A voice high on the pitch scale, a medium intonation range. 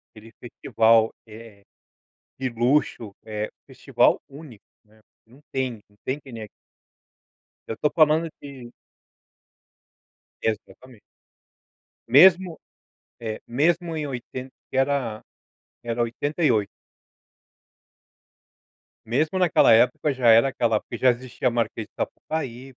No: low, 125 Hz; average, 4.1 semitones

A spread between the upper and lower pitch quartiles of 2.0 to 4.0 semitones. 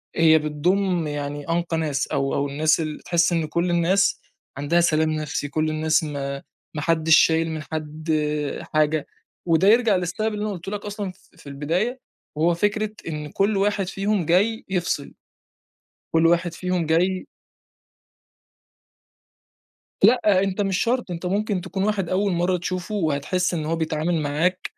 Yes: average, 3.7 semitones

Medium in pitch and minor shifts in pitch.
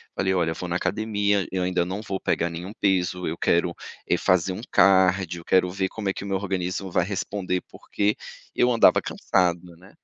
No: very low, 95 Hz; narrow, 1.8 semitones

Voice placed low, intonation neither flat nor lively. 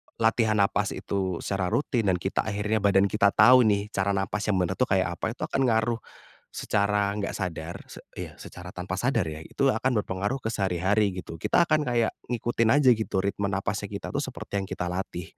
Yes: low, 100 Hz; average, 3.2 semitones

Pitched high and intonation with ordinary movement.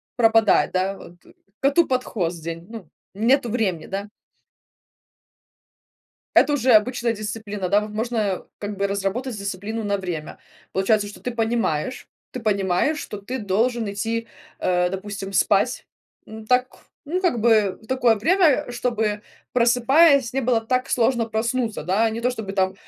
Yes: high, 220 Hz; average, 3.7 semitones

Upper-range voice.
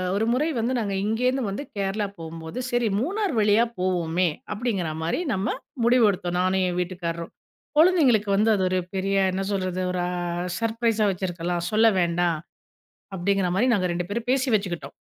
Yes: high, 195 Hz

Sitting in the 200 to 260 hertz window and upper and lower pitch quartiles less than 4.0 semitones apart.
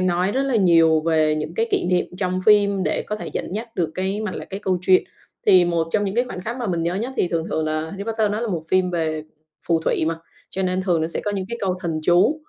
No: medium, 185 Hz; average, 3.6 semitones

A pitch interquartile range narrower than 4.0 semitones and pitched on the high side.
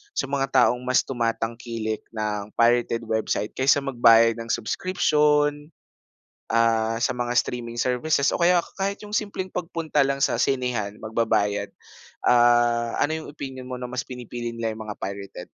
No: average, 3.3 semitones; low, 120 Hz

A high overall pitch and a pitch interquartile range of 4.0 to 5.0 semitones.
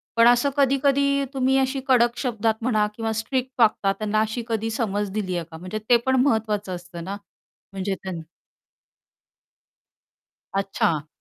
Yes: high, 220 Hz; average, 4.6 semitones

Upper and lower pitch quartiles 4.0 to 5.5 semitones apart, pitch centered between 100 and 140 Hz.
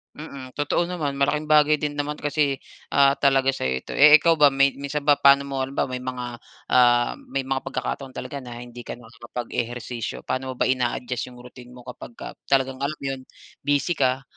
No: narrow, 2.4 semitones; low, 135 Hz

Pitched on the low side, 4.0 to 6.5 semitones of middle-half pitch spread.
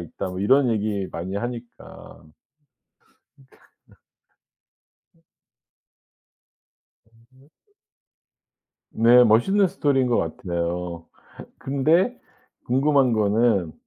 Yes: low, 120 Hz; wide, 5.5 semitones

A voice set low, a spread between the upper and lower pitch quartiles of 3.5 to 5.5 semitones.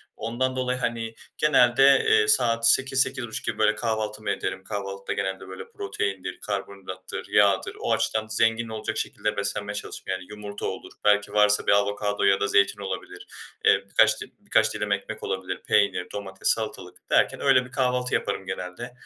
No: low, 105 Hz; average, 3.0 semitones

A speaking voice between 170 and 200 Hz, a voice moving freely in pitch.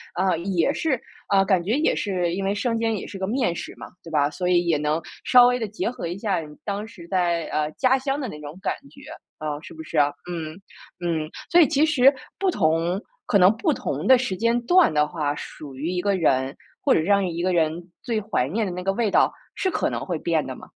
Yes: medium, 185 Hz; wide, 5.8 semitones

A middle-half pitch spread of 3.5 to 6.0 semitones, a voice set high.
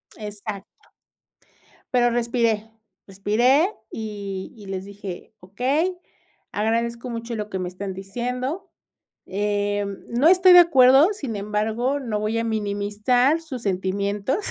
Yes: average, 3.9 semitones; high, 220 Hz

